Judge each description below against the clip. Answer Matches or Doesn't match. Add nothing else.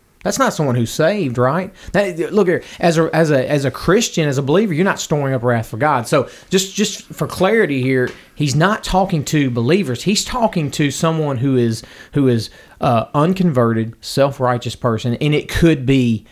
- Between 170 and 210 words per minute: Matches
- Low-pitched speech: Doesn't match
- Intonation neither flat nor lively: Doesn't match